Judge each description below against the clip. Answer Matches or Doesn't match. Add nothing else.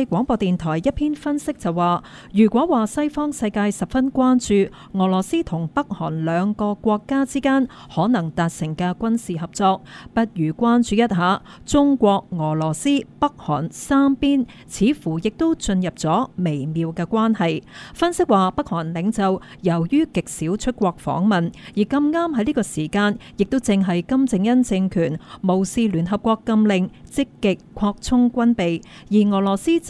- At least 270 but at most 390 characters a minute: Doesn't match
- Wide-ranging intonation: Matches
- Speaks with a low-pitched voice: Doesn't match